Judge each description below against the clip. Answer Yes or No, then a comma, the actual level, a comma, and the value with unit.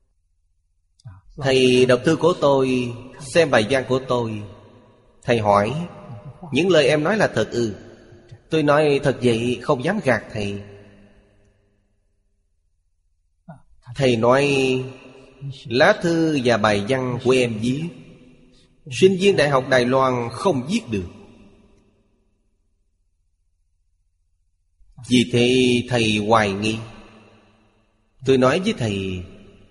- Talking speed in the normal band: No, slow, 115 wpm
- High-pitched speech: No, low, 115 Hz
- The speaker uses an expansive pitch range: No, average, 4.5 semitones